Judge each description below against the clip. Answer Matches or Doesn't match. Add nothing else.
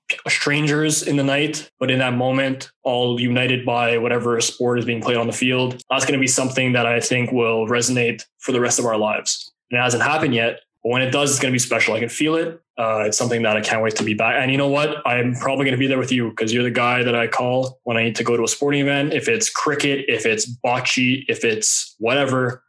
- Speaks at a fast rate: Matches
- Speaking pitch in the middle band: Doesn't match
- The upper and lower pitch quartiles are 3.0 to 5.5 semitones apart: Doesn't match